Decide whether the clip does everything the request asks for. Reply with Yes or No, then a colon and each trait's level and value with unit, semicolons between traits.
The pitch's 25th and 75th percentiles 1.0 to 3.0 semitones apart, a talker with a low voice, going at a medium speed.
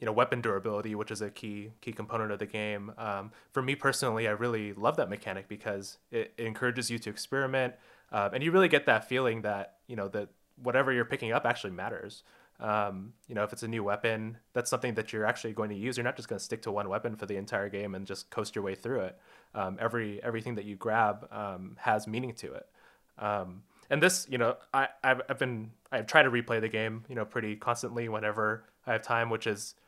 No: narrow, 2.6 semitones; low, 110 Hz; fast, 235 wpm